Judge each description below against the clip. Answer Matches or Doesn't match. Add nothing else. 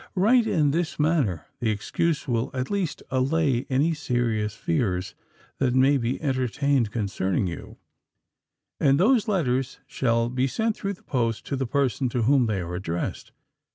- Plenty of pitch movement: Doesn't match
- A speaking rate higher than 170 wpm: Doesn't match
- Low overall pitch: Matches